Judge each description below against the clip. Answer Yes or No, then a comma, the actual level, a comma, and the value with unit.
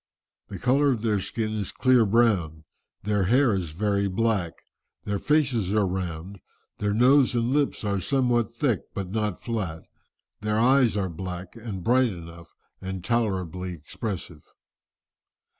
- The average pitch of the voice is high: No, low, 105 Hz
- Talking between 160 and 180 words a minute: No, average, 140 wpm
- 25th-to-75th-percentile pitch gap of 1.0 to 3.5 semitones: No, average, 4.3 semitones